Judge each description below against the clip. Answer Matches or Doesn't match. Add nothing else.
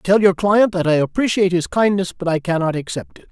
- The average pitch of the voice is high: Doesn't match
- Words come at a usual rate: Doesn't match